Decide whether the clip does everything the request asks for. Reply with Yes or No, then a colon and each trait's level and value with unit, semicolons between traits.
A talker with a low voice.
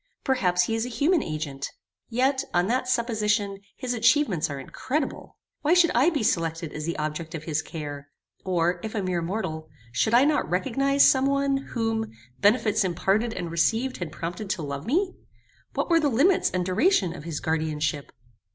No: high, 200 Hz